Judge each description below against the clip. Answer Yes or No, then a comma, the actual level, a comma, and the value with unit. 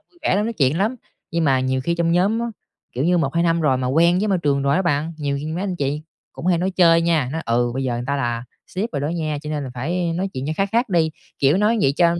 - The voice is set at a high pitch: No, medium, 165 Hz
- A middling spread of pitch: Yes, average, 4.4 semitones